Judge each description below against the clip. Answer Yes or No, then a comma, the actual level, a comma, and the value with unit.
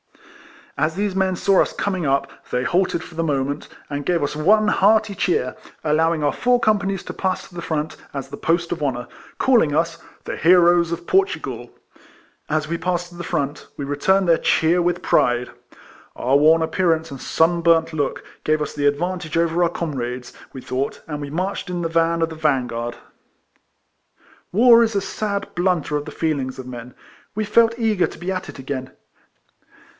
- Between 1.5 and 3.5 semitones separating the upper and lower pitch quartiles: No, average, 4.3 semitones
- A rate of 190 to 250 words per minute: Yes, average, 195 wpm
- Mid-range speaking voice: Yes, medium, 165 Hz